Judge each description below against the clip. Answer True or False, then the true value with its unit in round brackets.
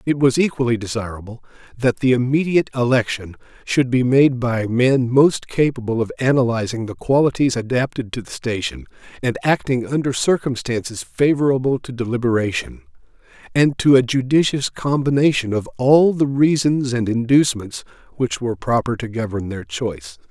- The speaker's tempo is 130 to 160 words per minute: True (140 wpm)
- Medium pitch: False (125 Hz)